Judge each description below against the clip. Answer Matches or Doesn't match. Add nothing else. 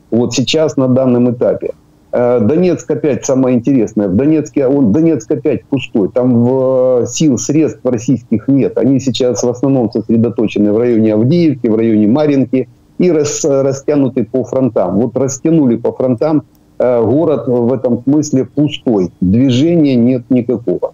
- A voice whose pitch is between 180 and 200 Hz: Doesn't match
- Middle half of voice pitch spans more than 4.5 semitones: Doesn't match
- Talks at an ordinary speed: Matches